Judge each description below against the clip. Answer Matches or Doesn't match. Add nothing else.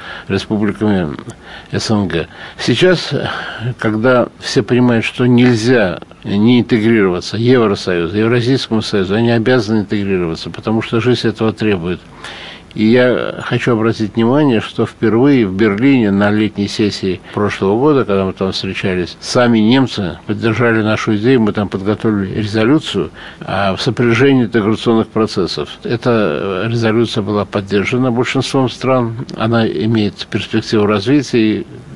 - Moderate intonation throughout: Matches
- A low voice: Matches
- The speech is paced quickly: Doesn't match